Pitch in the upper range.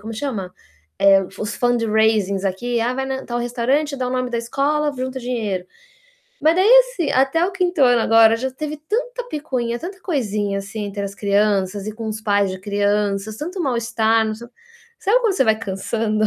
Yes: high, 235 Hz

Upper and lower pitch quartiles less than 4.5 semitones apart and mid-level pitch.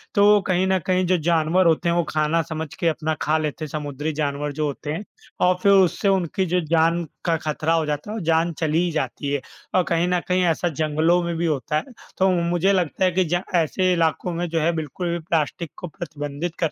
Yes: narrow, 2.5 semitones; medium, 165 Hz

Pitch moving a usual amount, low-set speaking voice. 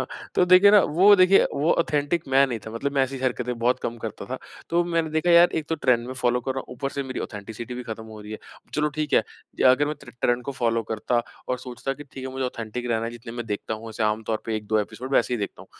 Yes: average, 3.7 semitones; low, 125 Hz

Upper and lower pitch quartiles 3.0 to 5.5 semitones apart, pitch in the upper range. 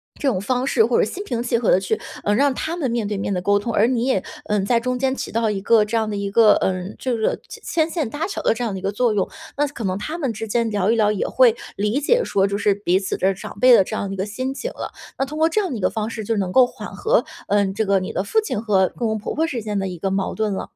Yes: average, 4.1 semitones; high, 220 Hz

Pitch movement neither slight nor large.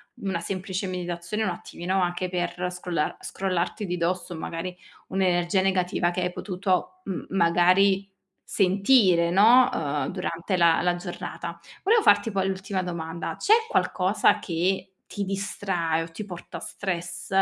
No: narrow, 1.9 semitones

